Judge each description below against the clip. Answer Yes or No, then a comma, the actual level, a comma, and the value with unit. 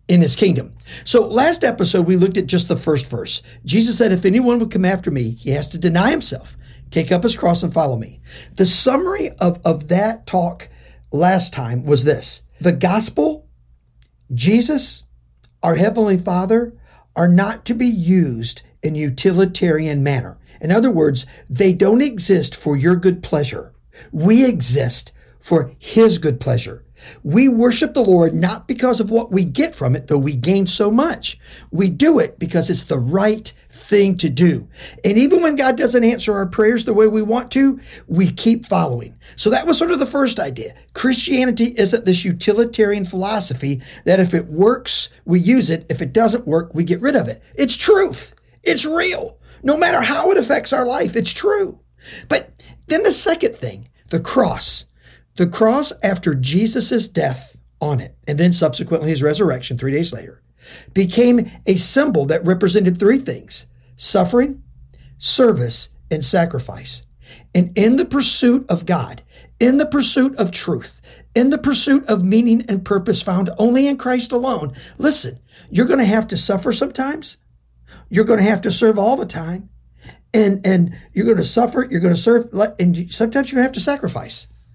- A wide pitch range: Yes, wide, 7.0 semitones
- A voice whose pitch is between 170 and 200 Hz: Yes, high, 190 Hz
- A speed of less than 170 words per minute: No, average, 175 wpm